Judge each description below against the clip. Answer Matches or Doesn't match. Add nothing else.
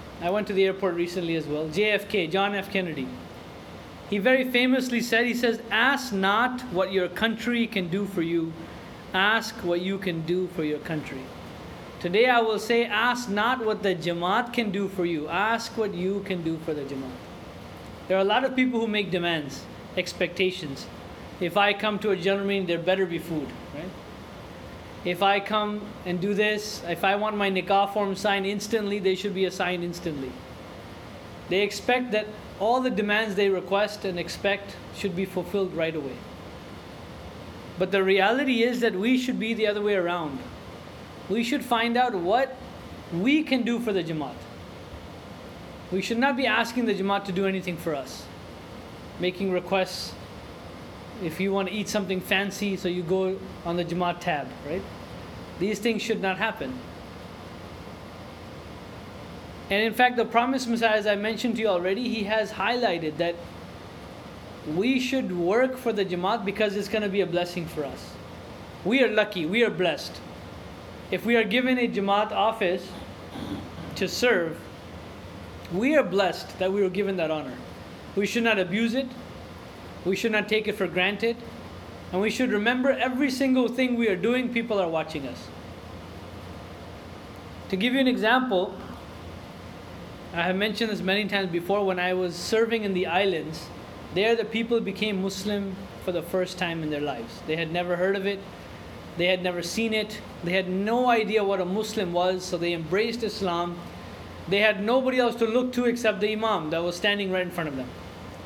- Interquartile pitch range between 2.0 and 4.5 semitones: Doesn't match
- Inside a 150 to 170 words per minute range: Doesn't match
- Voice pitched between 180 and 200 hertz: Matches